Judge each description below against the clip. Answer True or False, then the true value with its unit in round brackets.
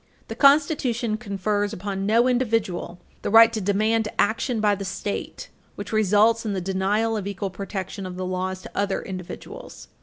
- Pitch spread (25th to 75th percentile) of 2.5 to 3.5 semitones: True (2.9 semitones)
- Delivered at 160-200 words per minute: True (170 wpm)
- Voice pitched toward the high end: True (205 Hz)